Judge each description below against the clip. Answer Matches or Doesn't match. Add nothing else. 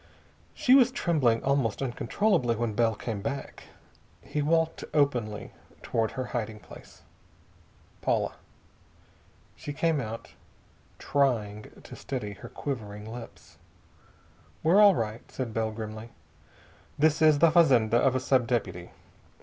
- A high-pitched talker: Doesn't match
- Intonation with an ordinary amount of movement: Matches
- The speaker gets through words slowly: Matches